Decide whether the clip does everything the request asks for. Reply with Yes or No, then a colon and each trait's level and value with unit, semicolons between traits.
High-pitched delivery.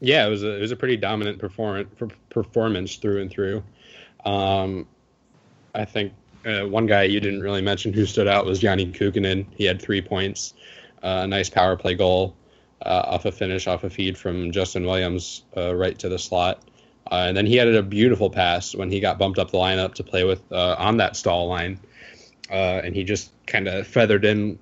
No: low, 100 Hz